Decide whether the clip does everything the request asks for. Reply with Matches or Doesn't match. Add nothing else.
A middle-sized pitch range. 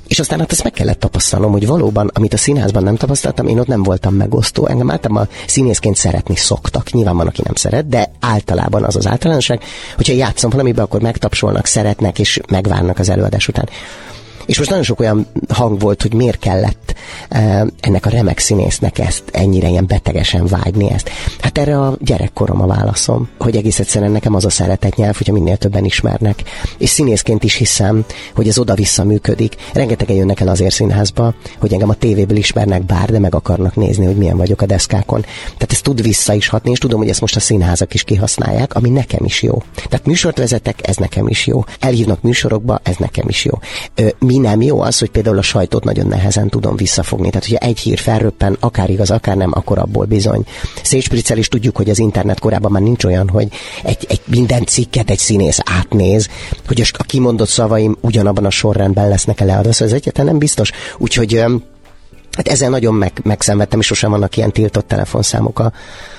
Matches